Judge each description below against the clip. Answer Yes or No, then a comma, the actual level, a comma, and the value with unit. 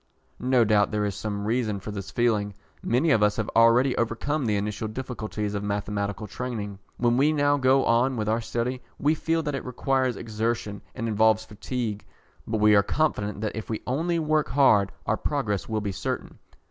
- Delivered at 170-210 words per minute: Yes, average, 190 wpm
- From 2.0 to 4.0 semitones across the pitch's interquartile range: Yes, average, 3.7 semitones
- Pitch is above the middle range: No, low, 110 Hz